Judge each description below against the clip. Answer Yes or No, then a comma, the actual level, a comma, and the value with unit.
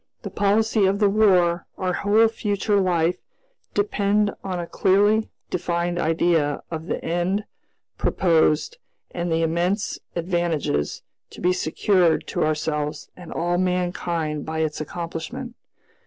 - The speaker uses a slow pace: Yes, slow, 125 wpm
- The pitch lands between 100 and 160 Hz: No, medium, 175 Hz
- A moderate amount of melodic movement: Yes, average, 3.6 semitones